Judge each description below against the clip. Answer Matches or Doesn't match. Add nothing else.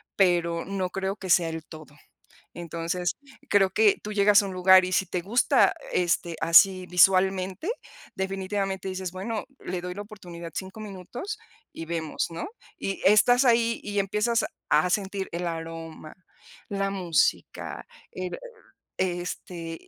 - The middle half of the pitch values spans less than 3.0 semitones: Matches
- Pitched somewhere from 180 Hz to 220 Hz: Matches